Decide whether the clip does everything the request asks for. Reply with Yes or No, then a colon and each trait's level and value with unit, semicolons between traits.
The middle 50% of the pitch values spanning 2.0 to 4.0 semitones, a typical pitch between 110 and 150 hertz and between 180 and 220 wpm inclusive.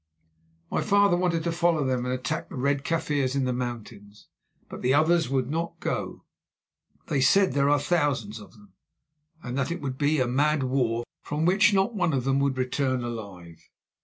No: average, 4.8 semitones; medium, 140 Hz; average, 190 wpm